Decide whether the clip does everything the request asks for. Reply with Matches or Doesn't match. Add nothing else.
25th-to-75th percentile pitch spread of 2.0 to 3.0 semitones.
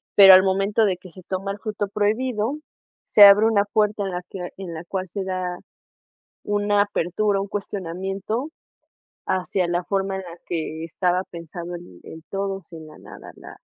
Matches